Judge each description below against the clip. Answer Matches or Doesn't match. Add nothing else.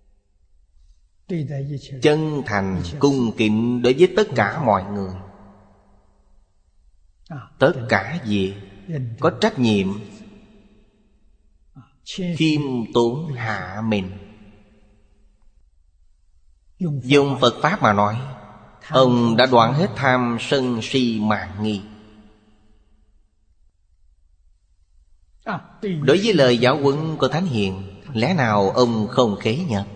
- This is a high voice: Doesn't match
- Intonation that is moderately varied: Doesn't match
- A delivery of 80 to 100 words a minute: Matches